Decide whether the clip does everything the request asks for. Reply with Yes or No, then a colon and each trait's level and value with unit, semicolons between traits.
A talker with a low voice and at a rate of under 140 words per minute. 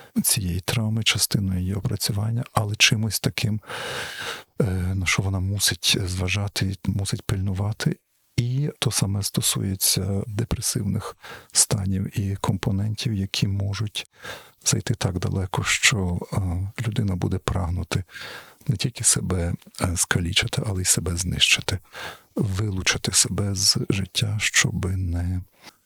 Yes: low, 100 Hz; slow, 105 wpm